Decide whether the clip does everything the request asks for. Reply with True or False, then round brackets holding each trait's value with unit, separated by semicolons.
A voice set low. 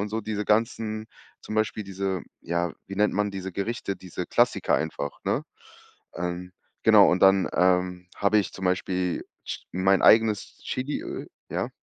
True (95 Hz)